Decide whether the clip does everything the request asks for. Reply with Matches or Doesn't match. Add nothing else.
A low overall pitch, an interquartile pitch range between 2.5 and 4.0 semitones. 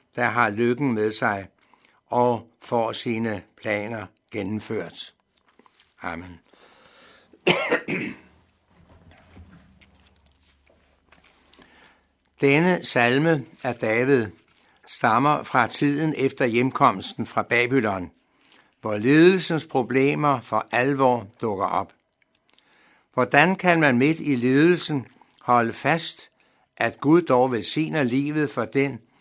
Doesn't match